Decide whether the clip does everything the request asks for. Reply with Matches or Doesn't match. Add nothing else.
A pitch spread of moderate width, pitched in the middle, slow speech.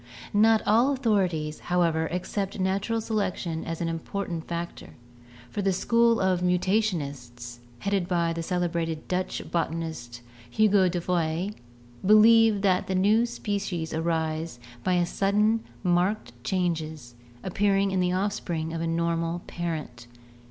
Matches